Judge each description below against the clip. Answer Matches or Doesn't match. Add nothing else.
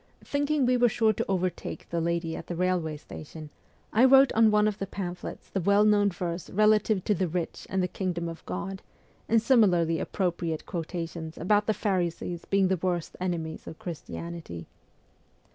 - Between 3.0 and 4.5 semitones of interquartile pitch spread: Matches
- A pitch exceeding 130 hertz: Matches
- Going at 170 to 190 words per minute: Matches